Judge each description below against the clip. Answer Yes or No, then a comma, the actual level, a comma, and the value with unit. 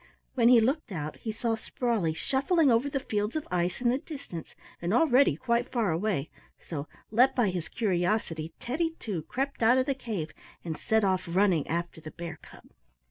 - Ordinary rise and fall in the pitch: No, wide, 6.7 semitones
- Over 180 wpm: Yes, average, 190 wpm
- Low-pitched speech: No, high, 220 Hz